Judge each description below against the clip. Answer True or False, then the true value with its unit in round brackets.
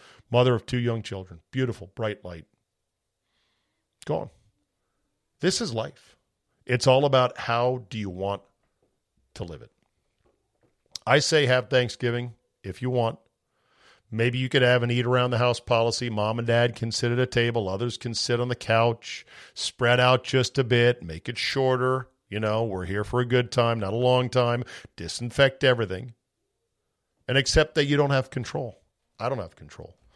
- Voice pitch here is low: True (120 Hz)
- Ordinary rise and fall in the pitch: False (2.0 semitones)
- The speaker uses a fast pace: False (175 wpm)